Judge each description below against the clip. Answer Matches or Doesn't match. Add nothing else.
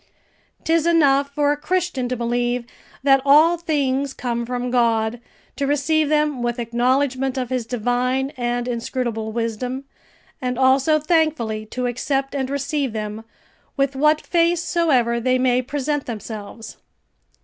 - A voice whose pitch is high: Matches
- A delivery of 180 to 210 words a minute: Doesn't match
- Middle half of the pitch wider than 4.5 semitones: Doesn't match